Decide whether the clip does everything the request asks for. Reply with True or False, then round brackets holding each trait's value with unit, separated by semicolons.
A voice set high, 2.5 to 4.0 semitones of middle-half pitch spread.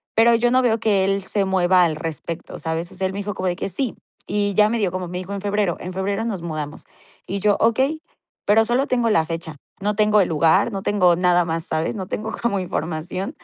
True (195 Hz; 3.3 semitones)